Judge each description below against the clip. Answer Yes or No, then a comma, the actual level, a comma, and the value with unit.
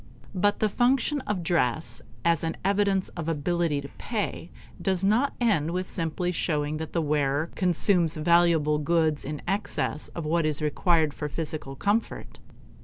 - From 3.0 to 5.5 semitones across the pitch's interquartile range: Yes, average, 4.0 semitones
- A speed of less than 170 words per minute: Yes, average, 155 wpm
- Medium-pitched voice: Yes, medium, 170 Hz